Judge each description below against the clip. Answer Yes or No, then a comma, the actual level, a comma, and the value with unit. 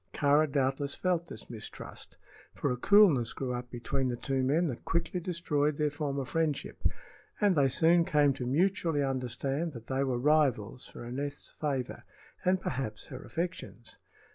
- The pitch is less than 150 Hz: Yes, medium, 140 Hz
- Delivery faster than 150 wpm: Yes, average, 160 wpm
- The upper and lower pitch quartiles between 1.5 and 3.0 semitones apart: No, average, 4.1 semitones